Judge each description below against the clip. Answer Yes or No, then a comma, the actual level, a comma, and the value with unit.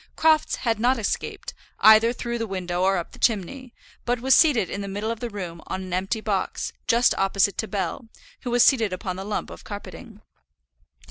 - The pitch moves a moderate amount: Yes, average, 3.7 semitones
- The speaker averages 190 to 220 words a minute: Yes, average, 200 wpm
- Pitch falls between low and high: No, high, 215 Hz